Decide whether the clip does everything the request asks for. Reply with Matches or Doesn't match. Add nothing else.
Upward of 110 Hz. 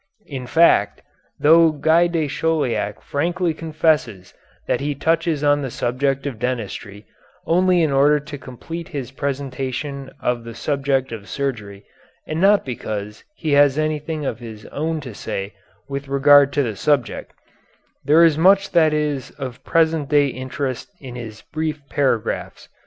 Matches